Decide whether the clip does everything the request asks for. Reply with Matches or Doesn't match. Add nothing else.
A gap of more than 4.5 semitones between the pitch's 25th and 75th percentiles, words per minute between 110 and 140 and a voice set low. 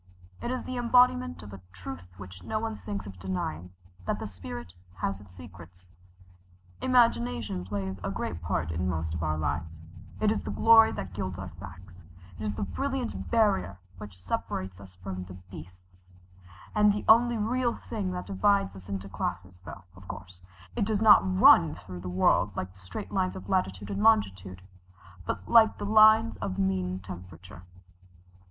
Doesn't match